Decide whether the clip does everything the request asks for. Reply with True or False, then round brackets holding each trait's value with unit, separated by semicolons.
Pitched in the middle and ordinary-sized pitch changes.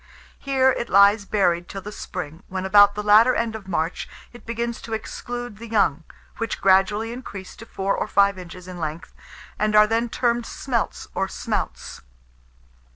False (205 Hz; 3.5 semitones)